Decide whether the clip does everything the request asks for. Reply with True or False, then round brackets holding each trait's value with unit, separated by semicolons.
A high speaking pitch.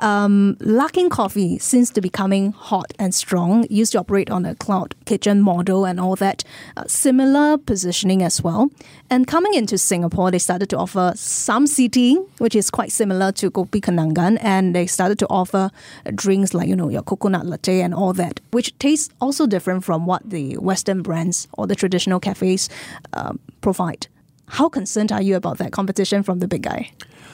True (195 Hz)